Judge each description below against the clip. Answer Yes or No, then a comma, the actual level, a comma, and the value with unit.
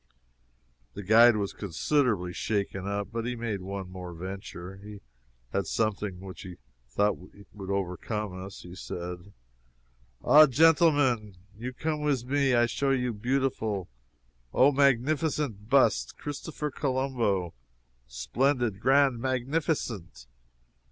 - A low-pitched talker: Yes, low, 110 Hz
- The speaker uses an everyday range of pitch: No, wide, 5.7 semitones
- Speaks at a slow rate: Yes, slow, 120 wpm